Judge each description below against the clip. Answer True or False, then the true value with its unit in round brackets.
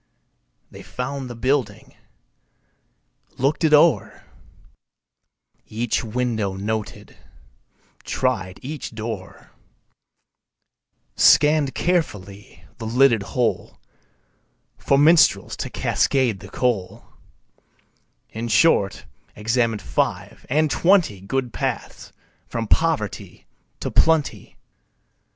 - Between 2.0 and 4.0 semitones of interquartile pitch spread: False (5.0 semitones)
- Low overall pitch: True (125 Hz)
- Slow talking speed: True (85 wpm)